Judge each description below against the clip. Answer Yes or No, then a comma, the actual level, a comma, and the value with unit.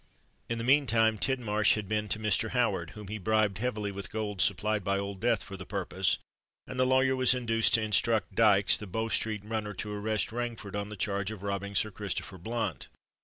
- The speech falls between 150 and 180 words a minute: No, fast, 205 wpm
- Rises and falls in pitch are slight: Yes, narrow, 2.2 semitones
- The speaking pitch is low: Yes, low, 105 Hz